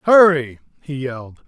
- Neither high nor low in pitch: Yes, medium, 145 Hz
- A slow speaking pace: Yes, slow, 120 wpm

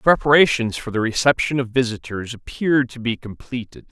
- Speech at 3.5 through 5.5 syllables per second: No, 5.7 syllables/s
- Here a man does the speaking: Yes, male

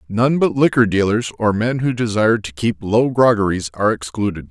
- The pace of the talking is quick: No, average, 185 wpm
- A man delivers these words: Yes, male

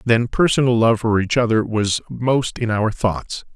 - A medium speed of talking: Yes, average, 185 wpm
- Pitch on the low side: Yes, low, 115 Hz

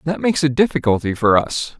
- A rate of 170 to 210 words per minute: Yes, average, 200 wpm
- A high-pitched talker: No, low, 135 Hz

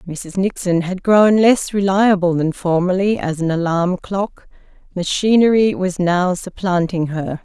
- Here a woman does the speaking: Yes, female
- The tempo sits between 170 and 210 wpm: No, slow, 135 wpm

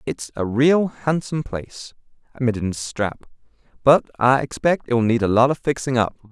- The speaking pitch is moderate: No, low, 125 Hz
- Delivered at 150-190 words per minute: Yes, average, 180 wpm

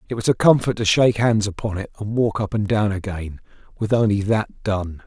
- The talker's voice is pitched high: No, low, 105 Hz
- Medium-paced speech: No, fast, 225 wpm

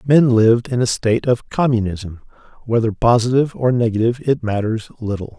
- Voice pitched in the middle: No, low, 115 Hz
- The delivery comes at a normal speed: Yes, average, 155 wpm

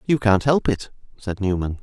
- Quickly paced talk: No, average, 195 wpm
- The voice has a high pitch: No, low, 105 Hz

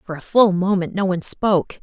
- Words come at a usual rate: No, fast, 230 wpm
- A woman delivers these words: Yes, female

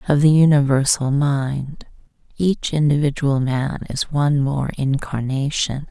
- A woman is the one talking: Yes, female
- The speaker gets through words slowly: Yes, slow, 110 wpm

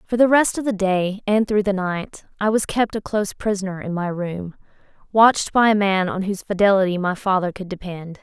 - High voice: Yes, high, 195 Hz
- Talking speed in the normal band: No, fast, 220 wpm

